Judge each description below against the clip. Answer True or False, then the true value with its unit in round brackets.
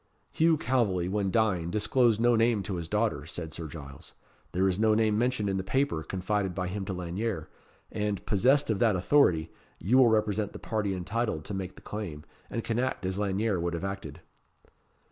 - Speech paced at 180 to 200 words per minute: True (195 wpm)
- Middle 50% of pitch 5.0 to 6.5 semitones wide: False (3.8 semitones)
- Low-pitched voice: True (100 Hz)